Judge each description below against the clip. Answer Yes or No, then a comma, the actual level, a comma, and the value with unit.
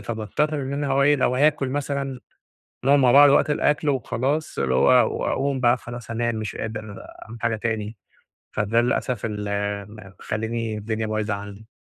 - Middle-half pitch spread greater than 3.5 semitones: Yes, average, 4.1 semitones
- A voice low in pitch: Yes, low, 120 Hz